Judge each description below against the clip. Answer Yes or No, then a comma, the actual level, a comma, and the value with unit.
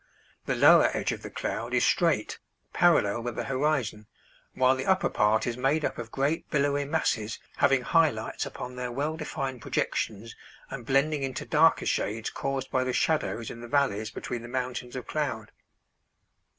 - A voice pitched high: No, low, 130 Hz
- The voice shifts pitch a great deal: No, average, 3.4 semitones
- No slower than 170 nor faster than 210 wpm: Yes, average, 175 wpm